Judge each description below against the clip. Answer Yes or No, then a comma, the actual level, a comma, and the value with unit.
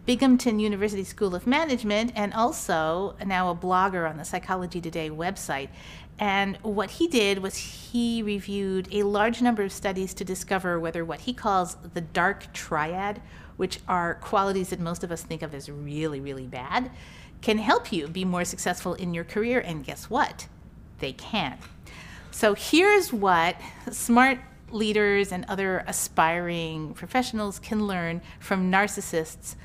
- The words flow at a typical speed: Yes, average, 155 wpm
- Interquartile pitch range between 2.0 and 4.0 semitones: Yes, average, 3.5 semitones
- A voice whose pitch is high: Yes, high, 195 Hz